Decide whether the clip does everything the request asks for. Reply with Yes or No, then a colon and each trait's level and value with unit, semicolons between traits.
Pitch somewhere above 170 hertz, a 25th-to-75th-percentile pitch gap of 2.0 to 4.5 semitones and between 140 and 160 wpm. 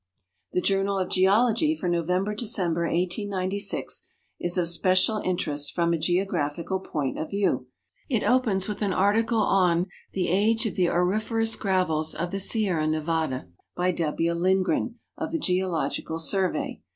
Yes: medium, 185 Hz; average, 3.2 semitones; average, 150 wpm